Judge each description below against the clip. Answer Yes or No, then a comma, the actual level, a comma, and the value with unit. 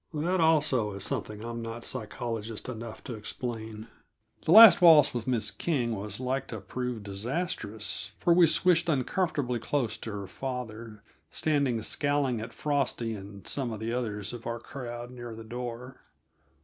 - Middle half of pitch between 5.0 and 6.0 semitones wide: No, average, 4.0 semitones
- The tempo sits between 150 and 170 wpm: Yes, average, 160 wpm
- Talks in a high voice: No, low, 120 Hz